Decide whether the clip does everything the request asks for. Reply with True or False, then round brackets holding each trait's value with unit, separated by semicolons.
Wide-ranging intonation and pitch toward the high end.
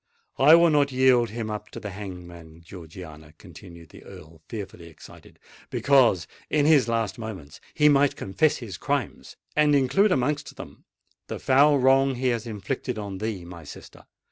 False (7.3 semitones; 110 Hz)